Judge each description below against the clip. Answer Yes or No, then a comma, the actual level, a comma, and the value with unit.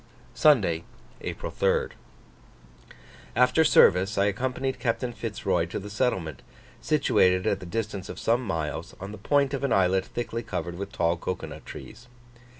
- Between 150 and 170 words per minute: Yes, average, 155 wpm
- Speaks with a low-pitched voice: Yes, low, 105 Hz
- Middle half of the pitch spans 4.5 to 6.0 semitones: Yes, average, 5.2 semitones